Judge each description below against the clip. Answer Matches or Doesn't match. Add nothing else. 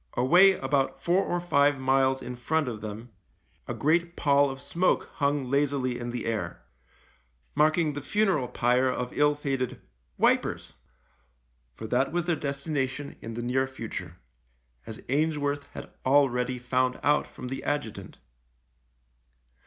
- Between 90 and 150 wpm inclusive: Matches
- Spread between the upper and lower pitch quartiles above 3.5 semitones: Doesn't match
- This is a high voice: Doesn't match